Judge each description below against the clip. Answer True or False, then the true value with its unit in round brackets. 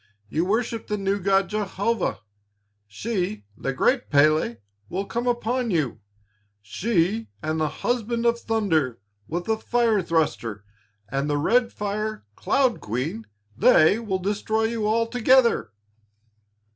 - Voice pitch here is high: True (205 Hz)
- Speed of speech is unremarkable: False (125 wpm)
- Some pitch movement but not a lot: False (6.6 semitones)